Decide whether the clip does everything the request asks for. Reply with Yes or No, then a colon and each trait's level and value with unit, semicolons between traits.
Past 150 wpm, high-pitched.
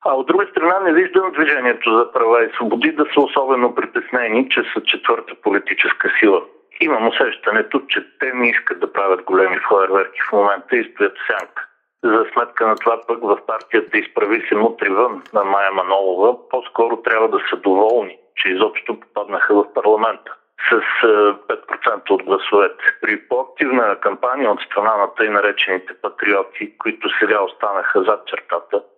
Yes: average, 160 wpm; very high, 340 Hz